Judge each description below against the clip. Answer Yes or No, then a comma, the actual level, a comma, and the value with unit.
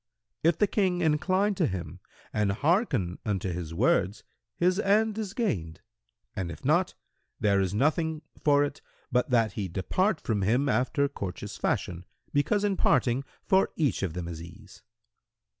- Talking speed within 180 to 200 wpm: No, average, 160 wpm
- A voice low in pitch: Yes, low, 125 Hz